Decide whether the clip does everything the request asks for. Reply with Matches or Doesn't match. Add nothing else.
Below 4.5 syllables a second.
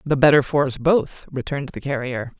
Doesn't match